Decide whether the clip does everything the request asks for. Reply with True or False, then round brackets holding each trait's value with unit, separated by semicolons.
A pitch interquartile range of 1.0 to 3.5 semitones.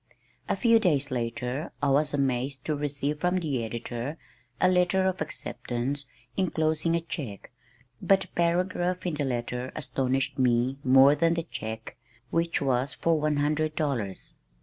False (4.5 semitones)